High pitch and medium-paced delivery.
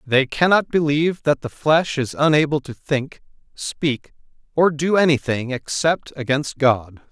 No: medium, 145 Hz; average, 145 wpm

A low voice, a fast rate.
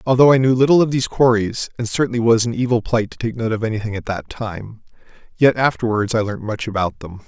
Yes: low, 115 Hz; fast, 230 wpm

